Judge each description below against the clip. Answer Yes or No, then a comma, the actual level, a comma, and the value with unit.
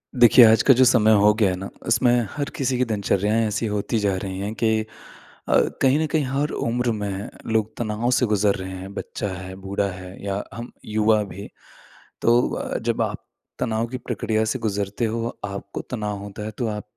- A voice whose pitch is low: Yes, low, 110 Hz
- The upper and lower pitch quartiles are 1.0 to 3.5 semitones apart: Yes, average, 2.8 semitones